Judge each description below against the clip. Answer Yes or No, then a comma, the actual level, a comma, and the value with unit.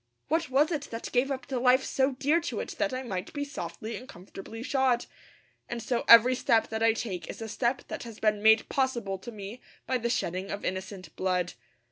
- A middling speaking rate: No, fast, 215 wpm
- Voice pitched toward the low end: No, high, 235 Hz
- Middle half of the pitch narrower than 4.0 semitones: No, average, 4.3 semitones